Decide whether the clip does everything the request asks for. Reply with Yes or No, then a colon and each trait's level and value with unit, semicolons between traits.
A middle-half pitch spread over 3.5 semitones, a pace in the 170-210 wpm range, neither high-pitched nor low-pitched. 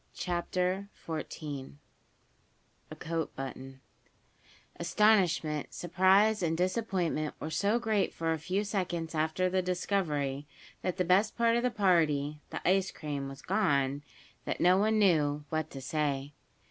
No: average, 4.4 semitones; slow, 135 wpm; medium, 170 Hz